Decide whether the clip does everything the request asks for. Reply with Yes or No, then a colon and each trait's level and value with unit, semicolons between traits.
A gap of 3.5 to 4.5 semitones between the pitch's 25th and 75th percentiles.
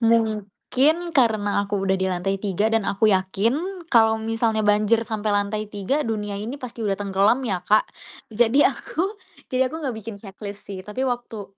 No: narrow, 2.5 semitones